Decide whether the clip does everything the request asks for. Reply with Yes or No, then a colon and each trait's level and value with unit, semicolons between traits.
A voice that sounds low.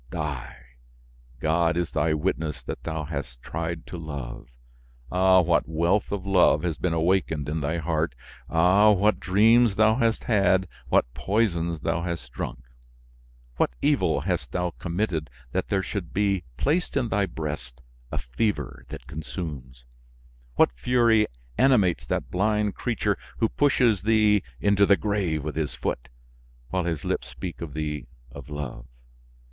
Yes: very low, 85 Hz